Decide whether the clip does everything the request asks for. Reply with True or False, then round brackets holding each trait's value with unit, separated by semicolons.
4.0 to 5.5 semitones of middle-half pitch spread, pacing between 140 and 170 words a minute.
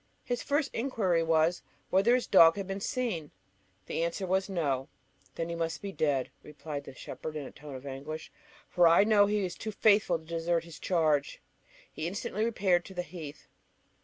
False (4.3 semitones; 190 wpm)